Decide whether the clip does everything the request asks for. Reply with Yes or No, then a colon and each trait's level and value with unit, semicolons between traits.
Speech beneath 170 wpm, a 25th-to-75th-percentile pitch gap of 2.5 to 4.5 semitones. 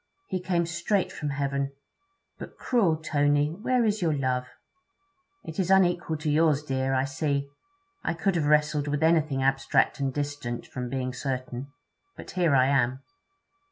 Yes: average, 160 wpm; average, 3.6 semitones